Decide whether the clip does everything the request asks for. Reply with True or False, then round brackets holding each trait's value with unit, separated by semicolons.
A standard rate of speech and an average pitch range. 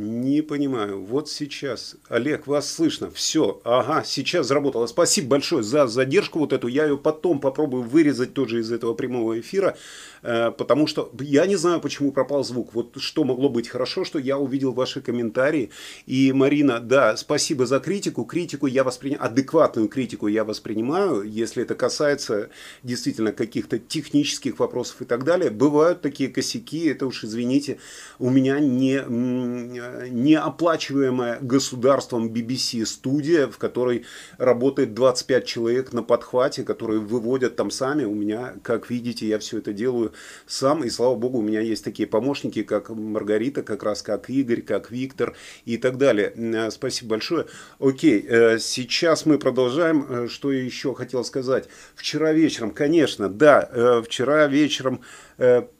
True (145 wpm; 3.4 semitones)